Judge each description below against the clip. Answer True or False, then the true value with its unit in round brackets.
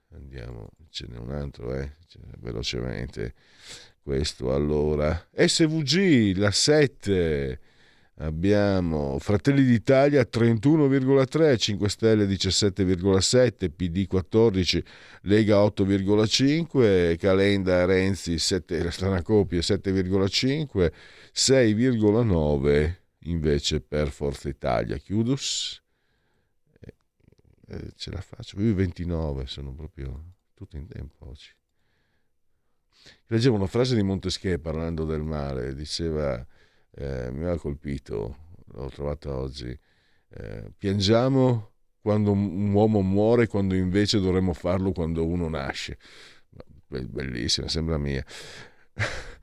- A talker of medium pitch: False (95 Hz)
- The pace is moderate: False (95 wpm)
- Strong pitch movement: True (5.9 semitones)